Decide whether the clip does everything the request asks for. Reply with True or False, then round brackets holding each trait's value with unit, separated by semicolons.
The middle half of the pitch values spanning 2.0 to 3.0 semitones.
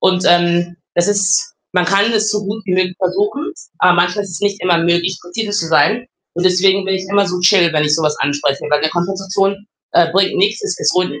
True (2.5 semitones)